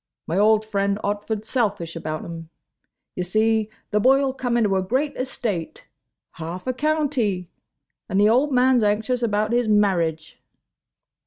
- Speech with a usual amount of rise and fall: Yes, average, 4.6 semitones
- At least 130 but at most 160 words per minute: Yes, average, 150 wpm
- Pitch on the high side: Yes, high, 215 Hz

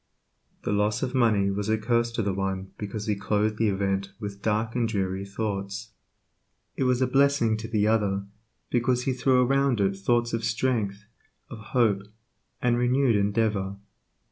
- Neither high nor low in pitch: No, low, 110 Hz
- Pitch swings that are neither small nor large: Yes, average, 3.2 semitones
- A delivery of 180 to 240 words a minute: No, average, 170 wpm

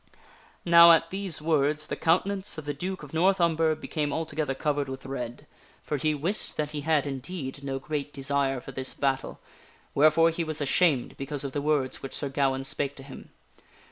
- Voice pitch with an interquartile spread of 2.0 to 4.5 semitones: Yes, average, 3.0 semitones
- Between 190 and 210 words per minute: Yes, average, 195 wpm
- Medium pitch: Yes, medium, 145 Hz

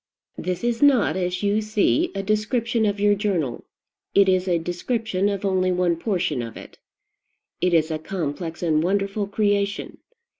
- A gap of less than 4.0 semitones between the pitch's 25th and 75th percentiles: Yes, average, 3.1 semitones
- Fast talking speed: No, average, 160 wpm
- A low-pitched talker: No, high, 195 Hz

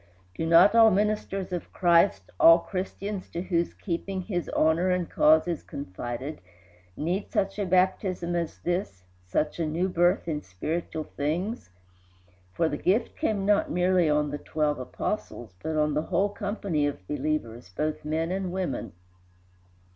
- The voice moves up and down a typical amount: Yes, average, 3.7 semitones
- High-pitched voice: No, medium, 170 Hz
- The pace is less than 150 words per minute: No, average, 155 wpm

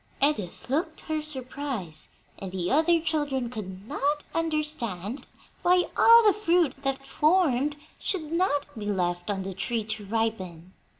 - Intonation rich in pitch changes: Yes, wide, 7.4 semitones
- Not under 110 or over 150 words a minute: Yes, average, 140 wpm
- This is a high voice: Yes, very high, 270 Hz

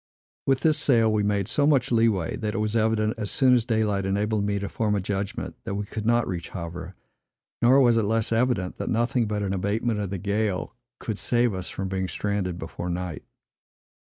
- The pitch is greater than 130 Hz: No, low, 105 Hz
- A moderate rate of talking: No, fast, 210 wpm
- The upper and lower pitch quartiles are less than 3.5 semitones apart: Yes, average, 2.9 semitones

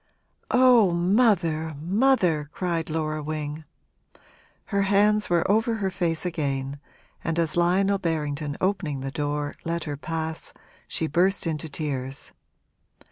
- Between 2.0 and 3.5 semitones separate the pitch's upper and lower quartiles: No, average, 4.3 semitones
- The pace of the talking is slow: Yes, slow, 125 wpm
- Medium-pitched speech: Yes, medium, 165 Hz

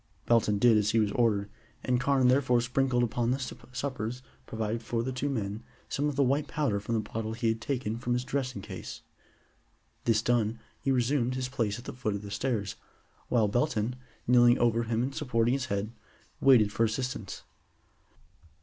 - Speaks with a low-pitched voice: Yes, low, 120 Hz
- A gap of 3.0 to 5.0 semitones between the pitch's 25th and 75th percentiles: No, narrow, 2.6 semitones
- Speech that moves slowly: No, average, 185 wpm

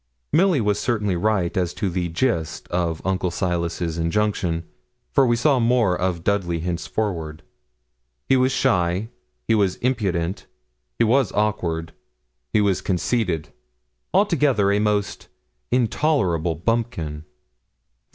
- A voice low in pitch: Yes, low, 100 Hz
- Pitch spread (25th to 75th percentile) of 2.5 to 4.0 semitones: No, average, 5.2 semitones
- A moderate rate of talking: No, slow, 120 wpm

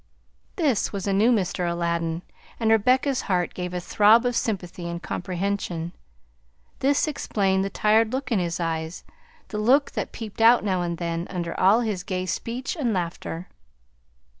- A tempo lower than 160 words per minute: No, average, 165 wpm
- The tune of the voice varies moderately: Yes, average, 4.6 semitones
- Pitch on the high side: Yes, high, 195 Hz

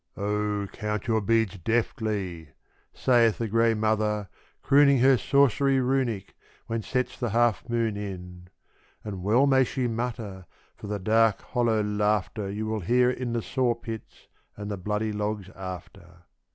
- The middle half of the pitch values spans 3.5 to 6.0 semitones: No, average, 2.7 semitones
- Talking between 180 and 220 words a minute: No, average, 145 wpm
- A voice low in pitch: Yes, low, 110 Hz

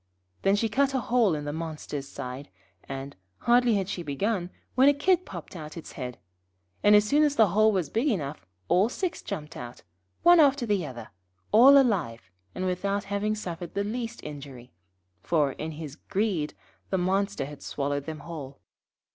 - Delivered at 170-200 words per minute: Yes, average, 180 wpm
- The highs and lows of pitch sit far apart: Yes, wide, 7.0 semitones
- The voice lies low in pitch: No, medium, 185 Hz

